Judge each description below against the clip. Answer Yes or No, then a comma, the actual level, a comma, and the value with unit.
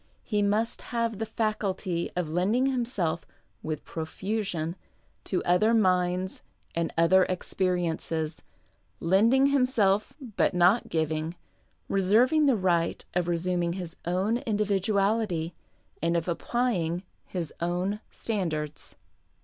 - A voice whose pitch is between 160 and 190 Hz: Yes, medium, 185 Hz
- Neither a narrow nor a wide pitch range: Yes, average, 4.2 semitones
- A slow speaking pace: Yes, slow, 110 wpm